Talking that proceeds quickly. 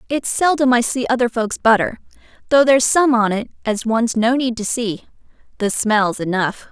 No: average, 180 wpm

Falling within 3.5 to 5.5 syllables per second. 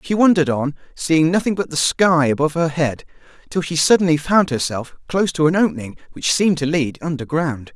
No: 5.9 syllables/s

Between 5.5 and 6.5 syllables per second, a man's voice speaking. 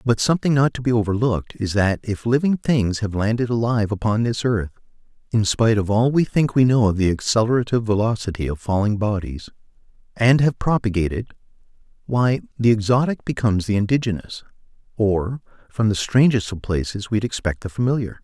Yes: 5.8 syllables/s; male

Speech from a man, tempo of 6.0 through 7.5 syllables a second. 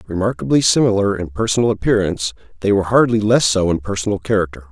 Yes: male; 6.9 syllables/s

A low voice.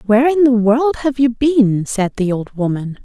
No: high, 235 Hz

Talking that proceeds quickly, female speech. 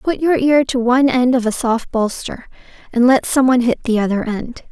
Yes: fast, 230 wpm; female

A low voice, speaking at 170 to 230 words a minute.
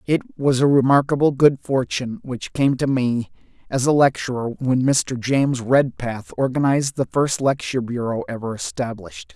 No: low, 130 Hz; average, 155 wpm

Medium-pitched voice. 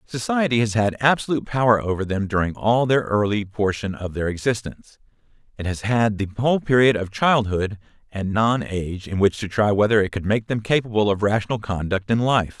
No: low, 110 Hz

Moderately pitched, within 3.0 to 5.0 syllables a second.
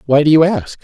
No: medium, 150 Hz; 5.9 syllables/s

